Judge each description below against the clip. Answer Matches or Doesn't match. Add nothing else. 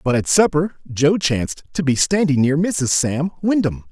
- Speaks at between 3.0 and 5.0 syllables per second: Matches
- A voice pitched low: Doesn't match